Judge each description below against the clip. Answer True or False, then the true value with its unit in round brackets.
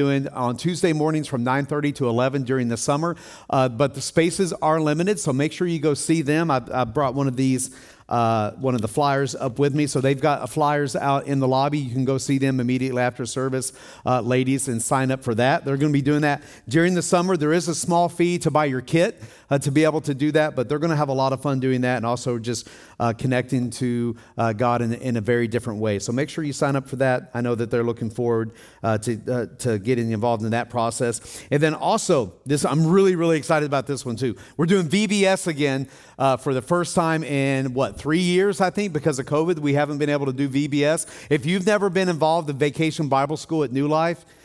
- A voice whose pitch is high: False (140 Hz)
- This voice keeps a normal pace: False (250 wpm)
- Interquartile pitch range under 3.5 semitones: False (3.8 semitones)